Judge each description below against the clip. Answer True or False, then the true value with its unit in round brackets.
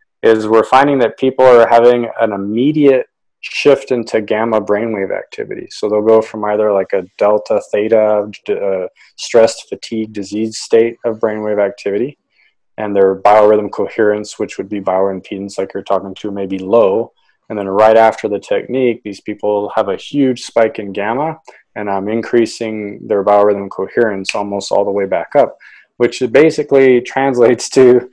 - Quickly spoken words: False (160 wpm)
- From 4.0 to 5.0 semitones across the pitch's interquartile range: False (3.5 semitones)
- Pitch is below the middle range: True (110 Hz)